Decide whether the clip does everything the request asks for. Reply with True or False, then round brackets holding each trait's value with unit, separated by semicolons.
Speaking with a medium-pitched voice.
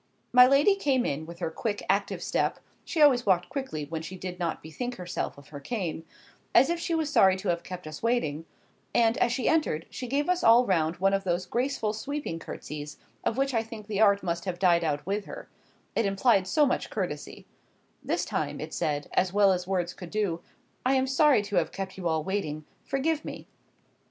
False (195 Hz)